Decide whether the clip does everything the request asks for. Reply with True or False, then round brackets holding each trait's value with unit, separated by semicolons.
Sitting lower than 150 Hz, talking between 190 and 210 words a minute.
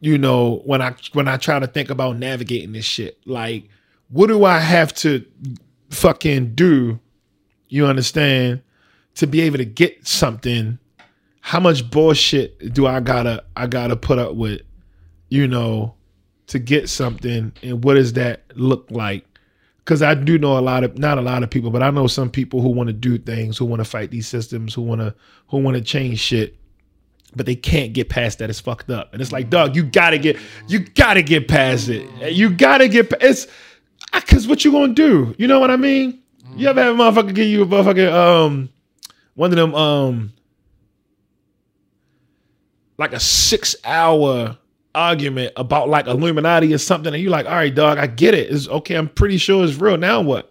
True (135 Hz; 195 wpm)